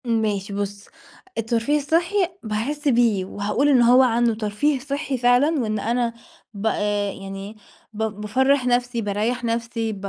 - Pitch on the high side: Yes, high, 230 Hz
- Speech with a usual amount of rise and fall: Yes, average, 3.3 semitones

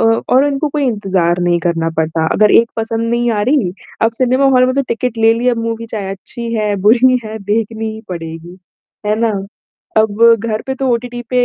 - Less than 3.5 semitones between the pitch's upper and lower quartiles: Yes, average, 3.0 semitones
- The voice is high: Yes, high, 225 Hz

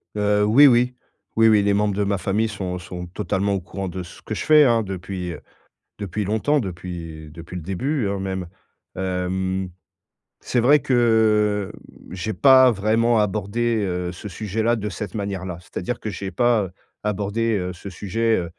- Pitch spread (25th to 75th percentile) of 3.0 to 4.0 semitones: Yes, average, 3.3 semitones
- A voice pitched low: Yes, low, 100 Hz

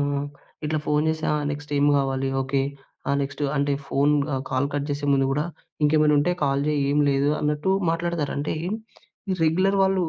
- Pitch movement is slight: Yes, narrow, 1.9 semitones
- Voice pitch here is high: No, medium, 145 Hz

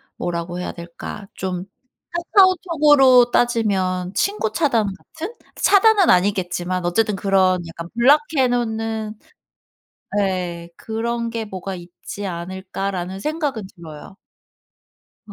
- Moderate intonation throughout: Yes, average, 5.0 semitones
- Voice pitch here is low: No, high, 205 Hz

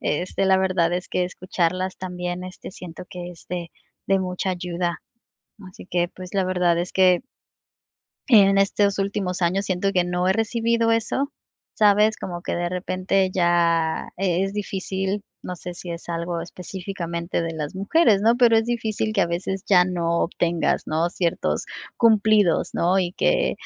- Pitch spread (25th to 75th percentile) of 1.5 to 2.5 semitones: Yes, narrow, 2.2 semitones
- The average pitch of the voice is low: No, medium, 185 Hz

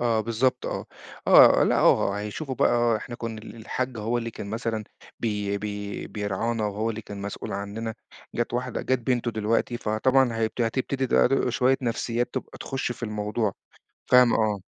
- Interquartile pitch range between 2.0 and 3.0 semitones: Yes, narrow, 2.4 semitones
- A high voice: No, low, 115 Hz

